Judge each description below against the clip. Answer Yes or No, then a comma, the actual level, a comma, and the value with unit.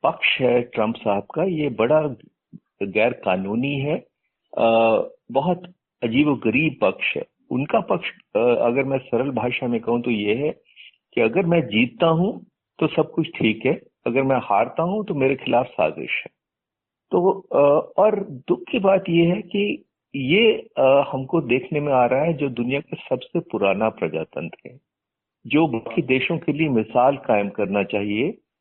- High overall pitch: No, medium, 140 Hz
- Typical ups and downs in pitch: No, wide, 6.3 semitones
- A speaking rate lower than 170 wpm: Yes, average, 160 wpm